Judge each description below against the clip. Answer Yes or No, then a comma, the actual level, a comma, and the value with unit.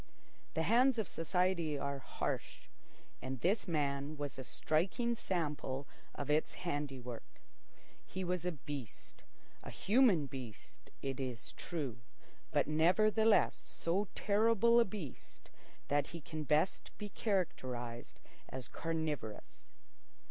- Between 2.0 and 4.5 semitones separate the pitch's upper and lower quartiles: No, wide, 5.5 semitones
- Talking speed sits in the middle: No, slow, 115 wpm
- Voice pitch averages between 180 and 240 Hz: No, medium, 155 Hz